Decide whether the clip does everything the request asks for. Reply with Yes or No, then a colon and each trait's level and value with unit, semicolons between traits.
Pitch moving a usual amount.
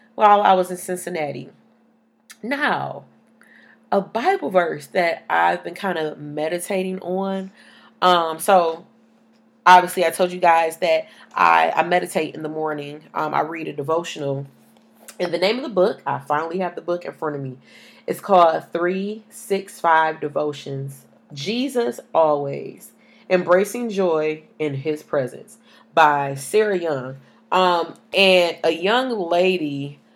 Yes: average, 4.6 semitones